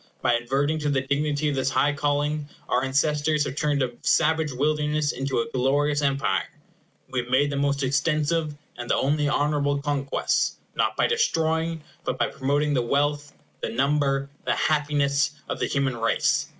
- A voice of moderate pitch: Yes, medium, 145 Hz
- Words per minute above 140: Yes, average, 170 wpm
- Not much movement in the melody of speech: Yes, narrow, 1.6 semitones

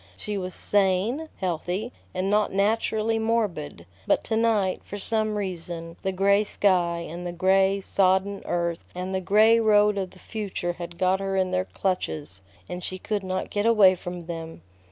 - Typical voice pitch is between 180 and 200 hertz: Yes, high, 190 Hz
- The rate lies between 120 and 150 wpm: No, average, 175 wpm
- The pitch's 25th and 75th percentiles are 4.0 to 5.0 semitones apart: No, average, 2.7 semitones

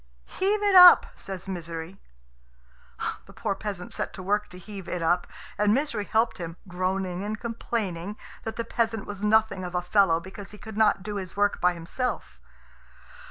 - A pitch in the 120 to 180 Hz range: No, high, 200 Hz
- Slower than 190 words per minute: Yes, average, 175 wpm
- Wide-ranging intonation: No, average, 3.4 semitones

